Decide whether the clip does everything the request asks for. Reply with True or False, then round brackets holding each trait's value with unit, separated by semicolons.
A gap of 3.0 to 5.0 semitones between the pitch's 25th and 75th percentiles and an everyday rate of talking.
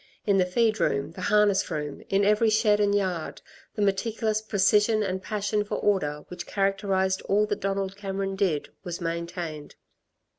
False (2.4 semitones; 160 wpm)